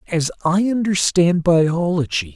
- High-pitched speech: No, medium, 170 Hz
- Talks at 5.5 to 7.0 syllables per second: No, 3.9 syllables/s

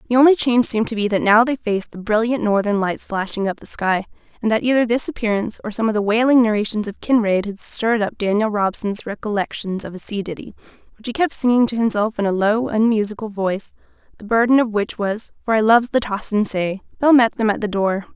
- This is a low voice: No, high, 215 Hz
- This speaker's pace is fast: Yes, fast, 230 wpm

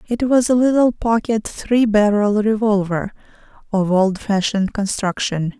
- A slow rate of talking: Yes, slow, 120 wpm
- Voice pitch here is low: No, high, 210 Hz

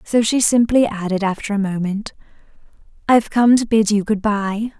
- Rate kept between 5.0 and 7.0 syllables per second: Yes, 5.1 syllables/s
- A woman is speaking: Yes, female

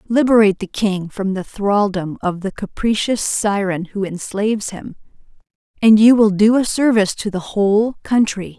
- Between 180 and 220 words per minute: No, average, 160 wpm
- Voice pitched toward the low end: No, high, 205 Hz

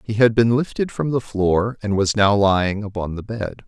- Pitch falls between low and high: No, low, 105 Hz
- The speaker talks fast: Yes, fast, 230 wpm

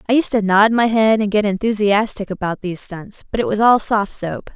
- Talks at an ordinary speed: No, fast, 235 wpm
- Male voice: No, female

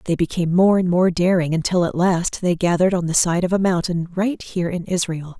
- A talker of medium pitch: Yes, medium, 175 Hz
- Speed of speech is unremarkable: No, fast, 235 wpm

